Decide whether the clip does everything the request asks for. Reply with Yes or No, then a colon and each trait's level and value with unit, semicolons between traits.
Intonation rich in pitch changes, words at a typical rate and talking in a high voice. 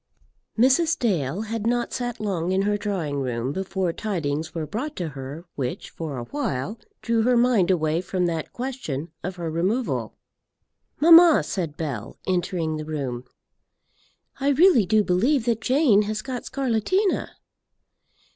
Yes: wide, 7.3 semitones; average, 145 wpm; high, 195 Hz